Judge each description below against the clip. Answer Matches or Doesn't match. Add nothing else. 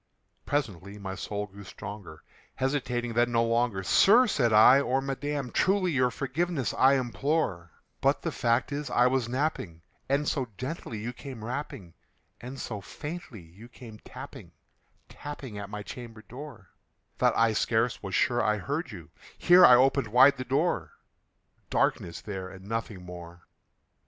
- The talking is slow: Doesn't match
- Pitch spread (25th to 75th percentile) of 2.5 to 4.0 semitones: Doesn't match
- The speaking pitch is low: Matches